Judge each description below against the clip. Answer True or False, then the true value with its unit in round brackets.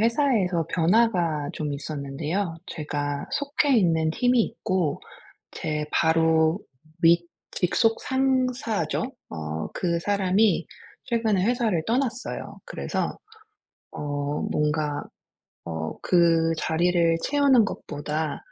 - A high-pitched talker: False (170 Hz)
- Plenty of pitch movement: True (6.7 semitones)